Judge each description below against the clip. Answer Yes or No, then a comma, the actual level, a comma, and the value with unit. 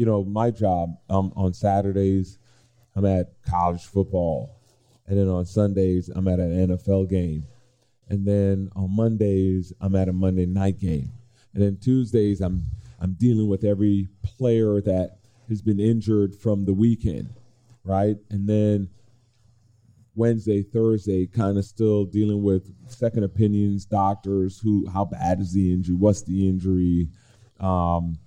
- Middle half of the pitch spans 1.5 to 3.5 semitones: Yes, average, 2.9 semitones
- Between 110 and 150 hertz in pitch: No, low, 100 Hz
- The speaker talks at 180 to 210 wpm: No, average, 145 wpm